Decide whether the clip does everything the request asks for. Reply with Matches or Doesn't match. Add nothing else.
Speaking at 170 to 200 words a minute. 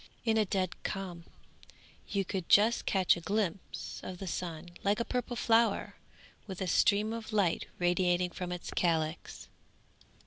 Doesn't match